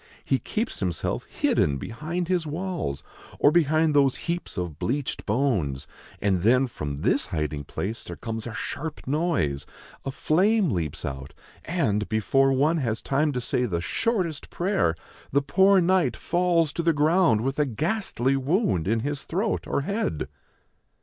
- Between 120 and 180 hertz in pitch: Yes, medium, 140 Hz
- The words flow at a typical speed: Yes, average, 155 wpm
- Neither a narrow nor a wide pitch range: No, wide, 8.0 semitones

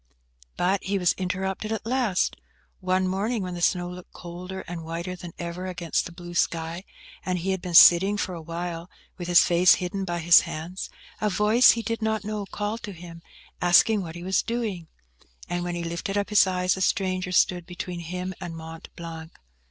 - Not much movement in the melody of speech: Yes, narrow, 2.2 semitones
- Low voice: No, medium, 180 Hz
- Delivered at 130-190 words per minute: No, average, 200 wpm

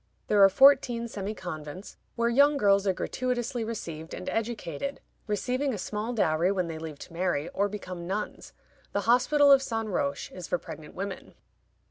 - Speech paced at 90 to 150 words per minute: No, average, 170 wpm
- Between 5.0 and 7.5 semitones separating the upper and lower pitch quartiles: Yes, average, 5.3 semitones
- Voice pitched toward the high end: Yes, high, 205 Hz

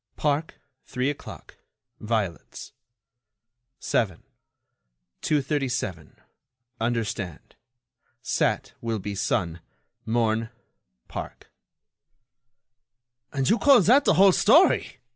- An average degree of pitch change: No, wide, 6.0 semitones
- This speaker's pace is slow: Yes, slow, 80 wpm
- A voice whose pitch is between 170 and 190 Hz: No, low, 115 Hz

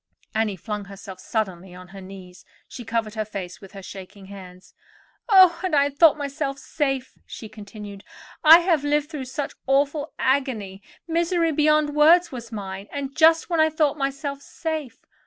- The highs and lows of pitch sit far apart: Yes, wide, 7.3 semitones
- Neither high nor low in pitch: No, very high, 270 Hz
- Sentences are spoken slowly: No, average, 160 wpm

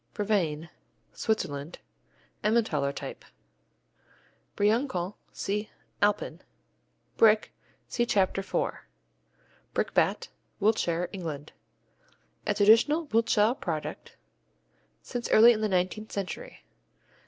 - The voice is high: Yes, high, 210 Hz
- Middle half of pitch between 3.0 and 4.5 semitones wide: Yes, average, 3.8 semitones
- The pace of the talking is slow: Yes, slow, 85 wpm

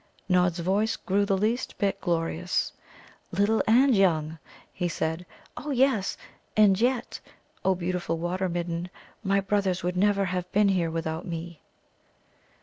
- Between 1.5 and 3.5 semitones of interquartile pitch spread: Yes, average, 2.8 semitones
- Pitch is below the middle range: No, medium, 185 Hz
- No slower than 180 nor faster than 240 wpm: No, average, 140 wpm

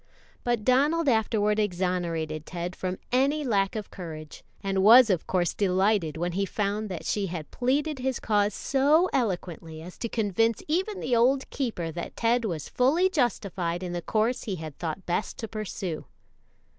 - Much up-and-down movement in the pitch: Yes, wide, 5.7 semitones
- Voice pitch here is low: No, high, 205 Hz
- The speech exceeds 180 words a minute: No, average, 170 wpm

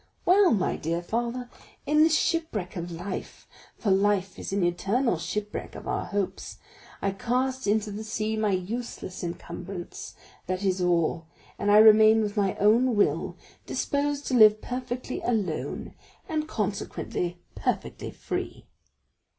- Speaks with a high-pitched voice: Yes, high, 210 Hz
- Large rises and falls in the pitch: No, average, 4.8 semitones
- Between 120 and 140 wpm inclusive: Yes, slow, 135 wpm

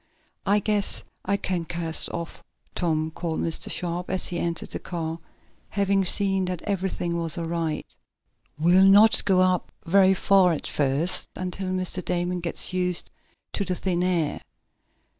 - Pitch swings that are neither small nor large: No, narrow, 2.1 semitones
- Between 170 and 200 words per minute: No, average, 155 wpm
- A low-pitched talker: No, medium, 180 Hz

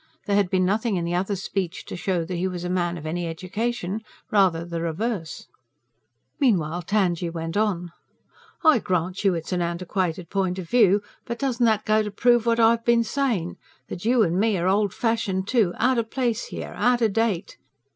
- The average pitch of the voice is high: Yes, high, 195 Hz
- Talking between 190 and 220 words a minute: Yes, average, 195 wpm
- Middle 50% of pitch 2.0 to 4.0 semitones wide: No, average, 4.4 semitones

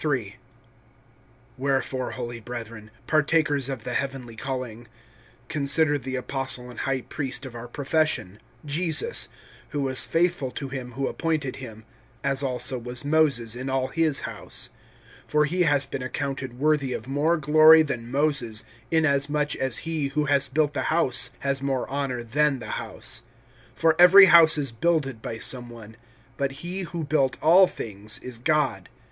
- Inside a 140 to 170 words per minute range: Yes, average, 155 wpm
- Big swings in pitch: No, average, 3.5 semitones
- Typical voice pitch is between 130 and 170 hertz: Yes, low, 135 Hz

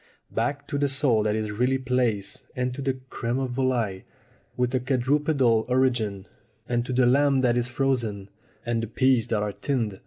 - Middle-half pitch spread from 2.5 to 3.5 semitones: Yes, average, 2.8 semitones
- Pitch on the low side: Yes, low, 125 Hz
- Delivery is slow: No, average, 185 wpm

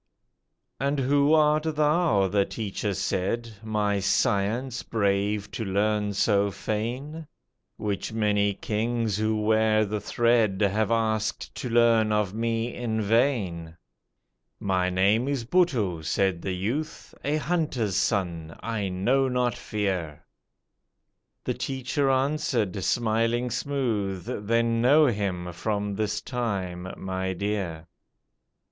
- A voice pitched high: No, low, 110 Hz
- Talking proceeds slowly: Yes, slow, 115 wpm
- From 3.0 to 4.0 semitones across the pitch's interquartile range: Yes, average, 3.5 semitones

